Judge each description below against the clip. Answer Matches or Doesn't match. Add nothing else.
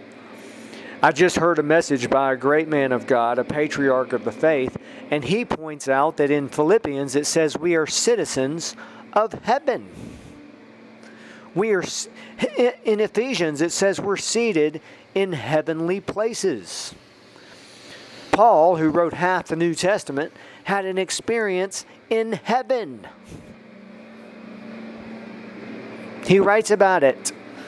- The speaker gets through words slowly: Matches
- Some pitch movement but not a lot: Doesn't match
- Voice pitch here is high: Doesn't match